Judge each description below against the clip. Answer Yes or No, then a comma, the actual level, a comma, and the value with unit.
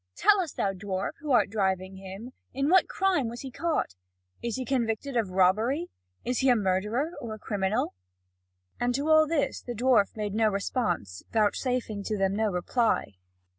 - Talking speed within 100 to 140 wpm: No, average, 175 wpm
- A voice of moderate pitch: No, high, 225 Hz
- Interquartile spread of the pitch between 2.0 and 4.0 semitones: No, average, 4.9 semitones